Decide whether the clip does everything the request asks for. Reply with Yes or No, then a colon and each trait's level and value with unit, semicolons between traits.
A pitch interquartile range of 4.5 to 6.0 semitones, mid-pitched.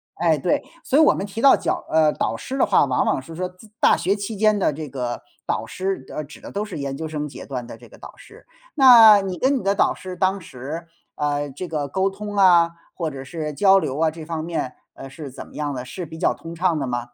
Yes: average, 5.1 semitones; medium, 165 Hz